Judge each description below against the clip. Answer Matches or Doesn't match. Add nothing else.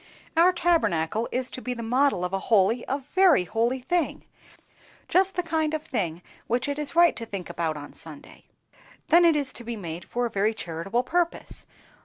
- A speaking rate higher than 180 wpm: Matches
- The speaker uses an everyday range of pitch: Doesn't match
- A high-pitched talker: Matches